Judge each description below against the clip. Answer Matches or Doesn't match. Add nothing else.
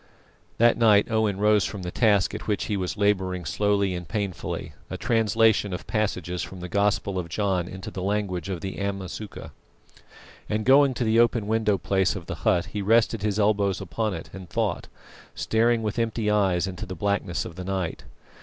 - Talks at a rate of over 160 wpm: Matches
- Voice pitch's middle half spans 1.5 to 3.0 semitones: Matches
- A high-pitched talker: Doesn't match